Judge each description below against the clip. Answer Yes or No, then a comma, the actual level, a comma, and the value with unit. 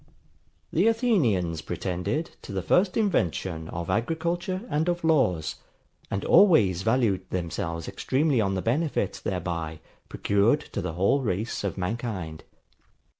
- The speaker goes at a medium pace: No, slow, 125 wpm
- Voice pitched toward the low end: Yes, low, 105 Hz